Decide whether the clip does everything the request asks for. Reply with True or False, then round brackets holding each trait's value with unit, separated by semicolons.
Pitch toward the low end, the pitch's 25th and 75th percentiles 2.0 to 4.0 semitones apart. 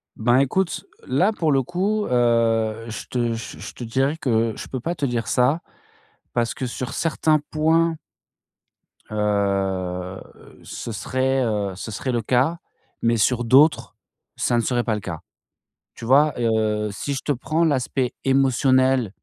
True (125 Hz; 3.7 semitones)